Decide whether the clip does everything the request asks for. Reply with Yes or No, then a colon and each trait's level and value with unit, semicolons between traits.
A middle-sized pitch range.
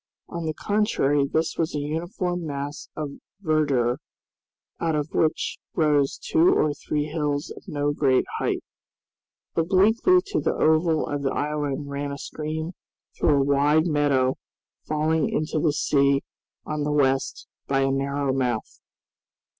No: narrow, 2.2 semitones